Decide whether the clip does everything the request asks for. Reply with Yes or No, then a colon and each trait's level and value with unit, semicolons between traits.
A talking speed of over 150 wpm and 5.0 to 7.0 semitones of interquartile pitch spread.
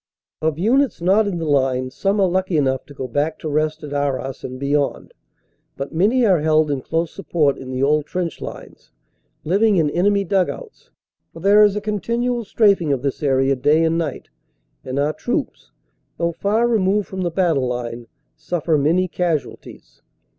Yes: average, 180 wpm; wide, 5.5 semitones